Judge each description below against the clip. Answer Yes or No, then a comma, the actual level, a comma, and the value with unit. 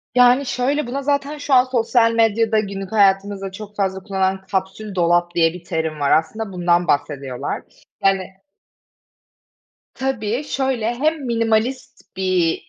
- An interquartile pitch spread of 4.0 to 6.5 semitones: Yes, average, 4.9 semitones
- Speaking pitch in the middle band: No, high, 210 Hz